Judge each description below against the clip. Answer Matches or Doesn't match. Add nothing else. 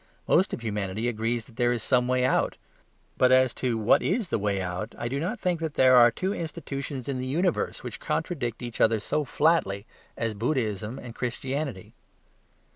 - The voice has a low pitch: Matches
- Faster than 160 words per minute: Matches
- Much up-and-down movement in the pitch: Doesn't match